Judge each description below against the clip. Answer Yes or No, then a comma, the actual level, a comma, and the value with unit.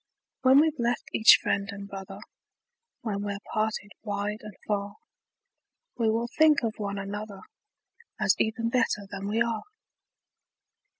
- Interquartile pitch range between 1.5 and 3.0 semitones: Yes, narrow, 2.5 semitones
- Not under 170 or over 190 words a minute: No, slow, 135 wpm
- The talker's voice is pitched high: Yes, high, 215 Hz